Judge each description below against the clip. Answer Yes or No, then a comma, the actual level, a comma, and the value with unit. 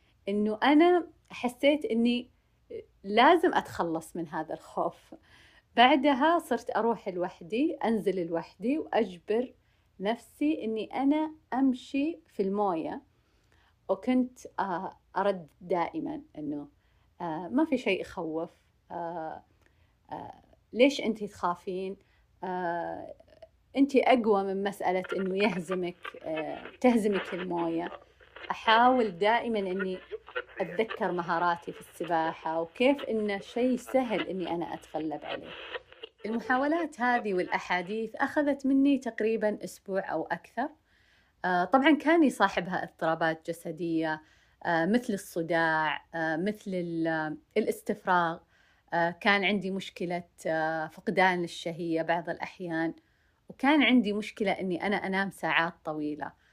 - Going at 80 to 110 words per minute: Yes, average, 95 wpm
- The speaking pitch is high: Yes, high, 200 Hz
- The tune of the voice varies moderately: No, wide, 6.5 semitones